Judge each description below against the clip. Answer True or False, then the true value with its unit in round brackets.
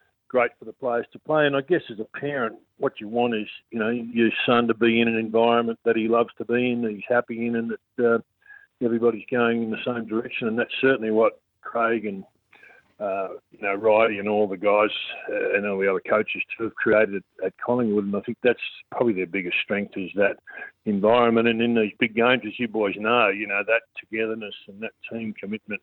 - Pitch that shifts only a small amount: True (2.1 semitones)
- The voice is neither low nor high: False (115 Hz)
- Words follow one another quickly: True (225 wpm)